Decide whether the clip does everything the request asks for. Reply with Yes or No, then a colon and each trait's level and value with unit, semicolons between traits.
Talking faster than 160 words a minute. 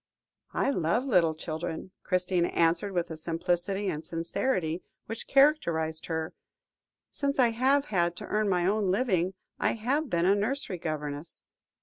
No: average, 145 wpm